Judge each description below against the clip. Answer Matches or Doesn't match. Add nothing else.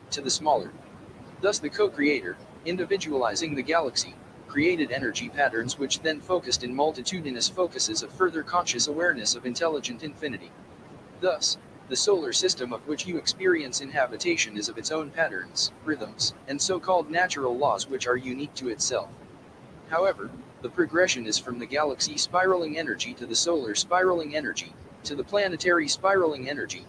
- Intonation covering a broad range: Matches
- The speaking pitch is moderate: Matches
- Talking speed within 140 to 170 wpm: Matches